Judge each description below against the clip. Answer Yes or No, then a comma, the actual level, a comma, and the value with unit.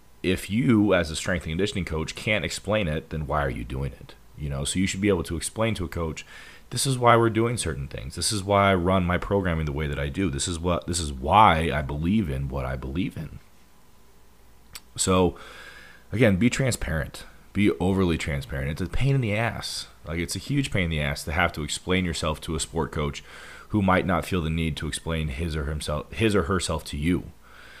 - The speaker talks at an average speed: No, fast, 230 wpm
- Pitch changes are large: No, average, 4.2 semitones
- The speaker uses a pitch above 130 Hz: No, very low, 85 Hz